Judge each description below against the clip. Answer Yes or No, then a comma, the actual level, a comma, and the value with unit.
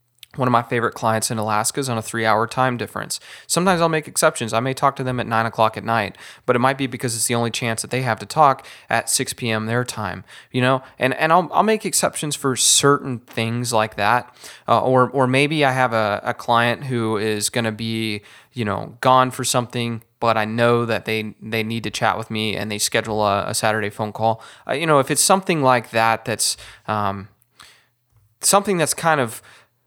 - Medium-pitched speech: No, low, 115 Hz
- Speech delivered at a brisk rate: Yes, fast, 225 wpm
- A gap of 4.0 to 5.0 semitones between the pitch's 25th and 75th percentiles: No, average, 2.8 semitones